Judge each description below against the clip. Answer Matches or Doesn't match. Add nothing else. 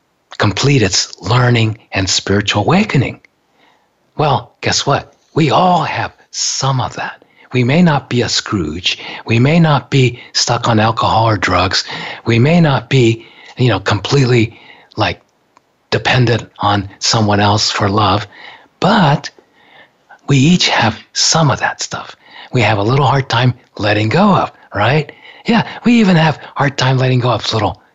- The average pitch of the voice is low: Matches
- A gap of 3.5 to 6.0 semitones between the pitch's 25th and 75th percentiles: Matches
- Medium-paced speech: Matches